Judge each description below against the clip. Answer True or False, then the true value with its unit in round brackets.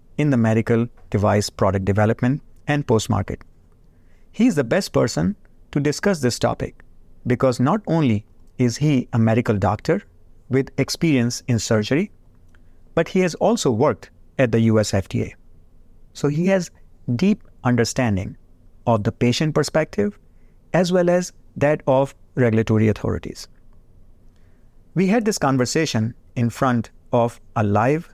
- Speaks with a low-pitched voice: True (120 Hz)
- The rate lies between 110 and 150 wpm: True (135 wpm)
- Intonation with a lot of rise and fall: True (5.9 semitones)